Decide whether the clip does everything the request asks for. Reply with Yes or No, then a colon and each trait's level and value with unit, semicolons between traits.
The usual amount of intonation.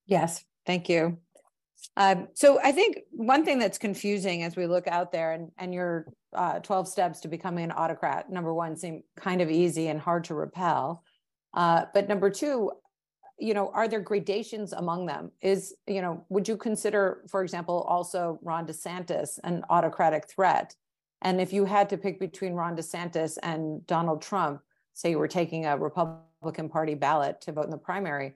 Yes: average, 3.2 semitones